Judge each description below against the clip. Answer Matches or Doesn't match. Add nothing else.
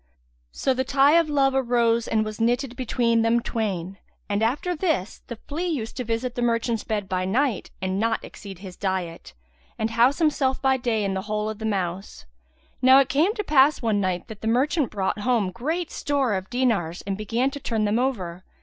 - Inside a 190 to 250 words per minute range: Matches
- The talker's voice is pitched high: Matches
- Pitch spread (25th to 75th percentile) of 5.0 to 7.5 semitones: Doesn't match